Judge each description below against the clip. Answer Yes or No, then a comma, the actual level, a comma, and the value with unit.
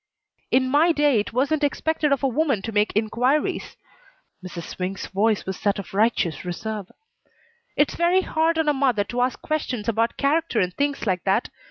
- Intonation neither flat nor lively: No, wide, 6.2 semitones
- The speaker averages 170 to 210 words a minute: Yes, average, 180 wpm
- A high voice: Yes, high, 245 Hz